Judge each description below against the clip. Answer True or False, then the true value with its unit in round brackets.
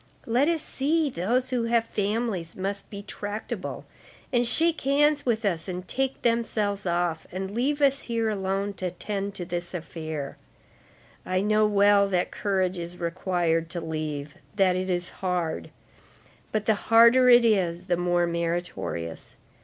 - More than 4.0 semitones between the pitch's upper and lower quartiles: True (4.8 semitones)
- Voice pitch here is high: True (195 Hz)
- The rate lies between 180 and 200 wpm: False (155 wpm)